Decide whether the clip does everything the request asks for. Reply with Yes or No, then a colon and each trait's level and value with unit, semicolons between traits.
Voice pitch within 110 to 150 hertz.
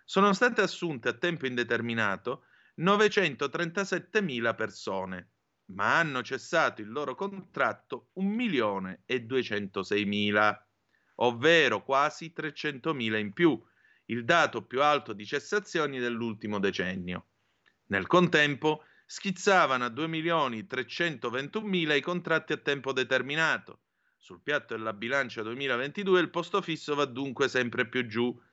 Yes: medium, 140 Hz